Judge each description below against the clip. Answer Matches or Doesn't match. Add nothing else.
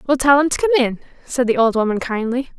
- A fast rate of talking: Matches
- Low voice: Doesn't match